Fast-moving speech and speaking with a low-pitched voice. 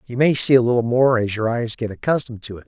Yes: fast, 290 wpm; low, 120 Hz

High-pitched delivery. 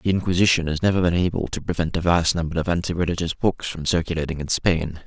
No: very low, 85 Hz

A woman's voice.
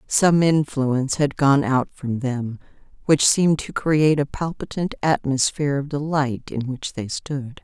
Yes: female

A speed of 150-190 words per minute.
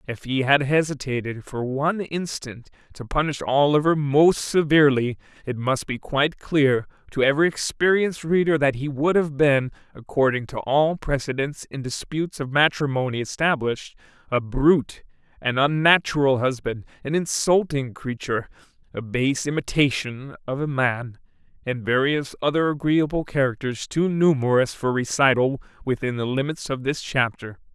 No: average, 140 wpm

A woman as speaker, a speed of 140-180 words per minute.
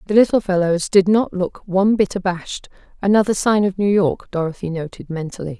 Yes: female; average, 170 wpm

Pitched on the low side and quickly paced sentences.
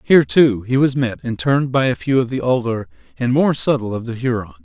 Yes: low, 120 Hz; fast, 245 wpm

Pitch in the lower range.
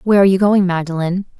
No: medium, 185 Hz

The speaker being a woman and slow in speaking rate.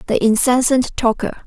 Yes: female; slow, 125 wpm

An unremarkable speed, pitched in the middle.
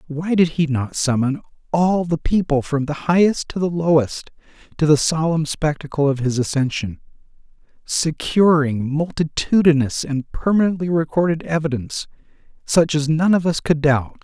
Yes: average, 145 wpm; medium, 155 Hz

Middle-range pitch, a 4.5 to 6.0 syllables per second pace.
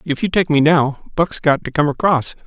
Yes: medium, 155 Hz; 5.1 syllables/s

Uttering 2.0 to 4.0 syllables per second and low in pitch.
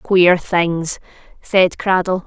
No: 2.7 syllables/s; medium, 180 Hz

